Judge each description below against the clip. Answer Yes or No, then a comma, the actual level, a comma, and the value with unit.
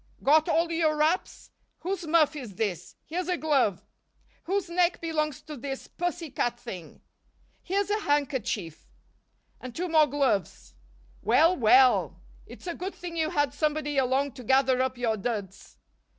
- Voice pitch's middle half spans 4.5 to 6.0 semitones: Yes, average, 5.0 semitones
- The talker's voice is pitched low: No, very high, 290 Hz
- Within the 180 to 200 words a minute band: No, average, 150 wpm